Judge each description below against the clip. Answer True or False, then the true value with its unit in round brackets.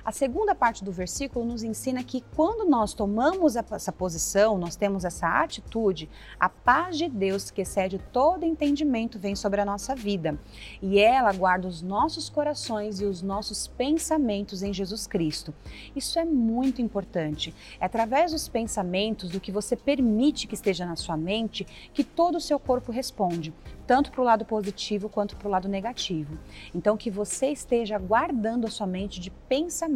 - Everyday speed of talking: True (170 wpm)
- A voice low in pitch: False (215 Hz)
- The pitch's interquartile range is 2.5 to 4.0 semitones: False (5.1 semitones)